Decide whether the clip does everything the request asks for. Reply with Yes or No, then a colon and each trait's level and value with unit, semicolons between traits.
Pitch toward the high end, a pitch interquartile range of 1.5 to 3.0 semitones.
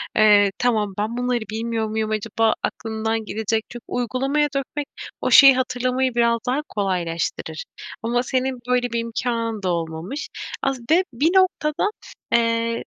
Yes: high, 235 Hz; average, 2.7 semitones